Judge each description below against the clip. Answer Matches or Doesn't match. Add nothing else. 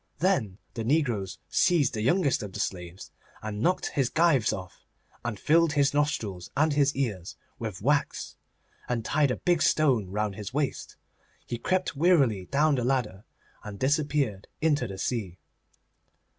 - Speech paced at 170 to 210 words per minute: Doesn't match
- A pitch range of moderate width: Doesn't match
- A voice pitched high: Doesn't match